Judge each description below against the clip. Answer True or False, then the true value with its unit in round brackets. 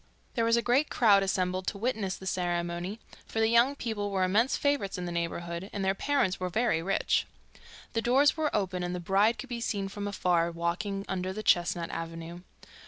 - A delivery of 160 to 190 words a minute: False (200 wpm)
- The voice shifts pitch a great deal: False (4.4 semitones)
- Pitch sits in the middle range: False (195 Hz)